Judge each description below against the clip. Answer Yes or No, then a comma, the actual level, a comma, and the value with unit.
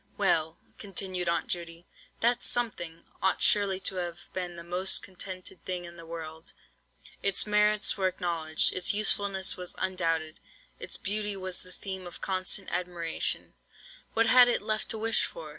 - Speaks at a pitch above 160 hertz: Yes, medium, 185 Hz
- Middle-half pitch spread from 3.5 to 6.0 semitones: No, average, 2.9 semitones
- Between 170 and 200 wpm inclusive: No, average, 160 wpm